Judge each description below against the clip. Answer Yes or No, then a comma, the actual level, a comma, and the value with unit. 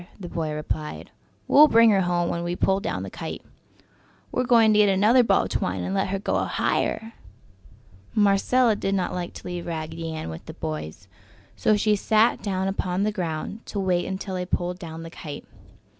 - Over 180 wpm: Yes, average, 195 wpm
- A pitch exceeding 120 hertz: Yes, high, 190 Hz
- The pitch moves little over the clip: No, average, 3.7 semitones